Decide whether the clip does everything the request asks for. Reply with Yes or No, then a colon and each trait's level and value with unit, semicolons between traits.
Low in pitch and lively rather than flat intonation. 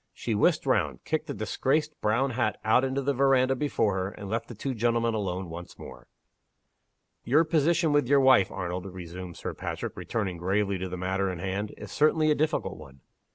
Yes: low, 110 Hz; wide, 6.4 semitones